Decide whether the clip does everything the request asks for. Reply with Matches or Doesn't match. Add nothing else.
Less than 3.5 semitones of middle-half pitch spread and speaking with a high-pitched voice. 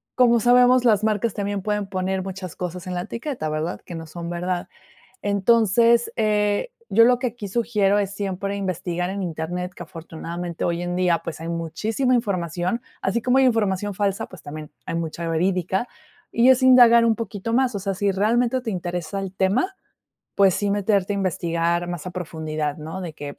Doesn't match